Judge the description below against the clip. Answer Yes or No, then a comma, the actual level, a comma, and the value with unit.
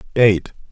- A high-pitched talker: No, low, 105 Hz